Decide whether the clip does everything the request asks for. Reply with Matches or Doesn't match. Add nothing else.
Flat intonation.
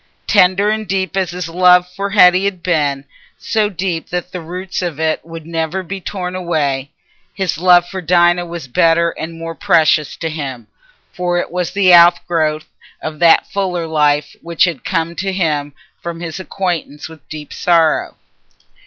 Matches